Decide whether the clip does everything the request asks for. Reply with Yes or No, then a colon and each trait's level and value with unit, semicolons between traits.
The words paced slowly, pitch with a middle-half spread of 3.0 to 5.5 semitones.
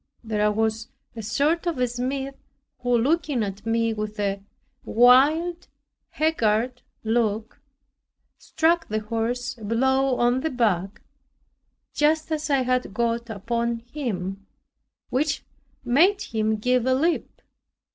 Yes: slow, 125 wpm; average, 3.9 semitones